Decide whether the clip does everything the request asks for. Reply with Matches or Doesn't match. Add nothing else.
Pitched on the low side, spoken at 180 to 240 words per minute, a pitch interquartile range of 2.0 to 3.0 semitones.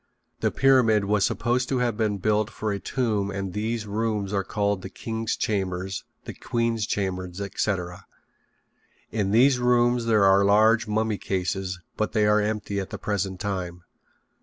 Doesn't match